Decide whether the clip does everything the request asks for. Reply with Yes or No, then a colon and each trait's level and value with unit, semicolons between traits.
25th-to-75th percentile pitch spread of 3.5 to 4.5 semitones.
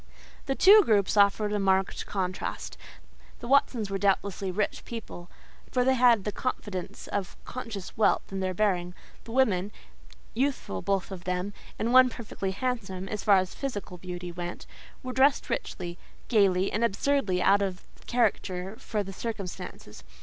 Yes: average, 4.0 semitones